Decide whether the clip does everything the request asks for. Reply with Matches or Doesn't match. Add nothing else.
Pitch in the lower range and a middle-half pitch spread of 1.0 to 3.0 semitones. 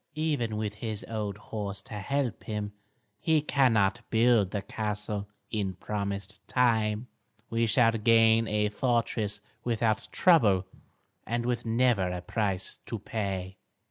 Matches